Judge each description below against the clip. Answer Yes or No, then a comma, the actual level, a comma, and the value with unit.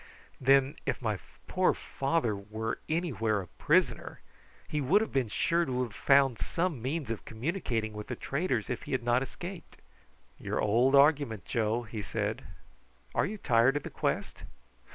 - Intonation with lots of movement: No, average, 4.7 semitones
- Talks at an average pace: Yes, average, 165 wpm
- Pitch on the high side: No, low, 130 Hz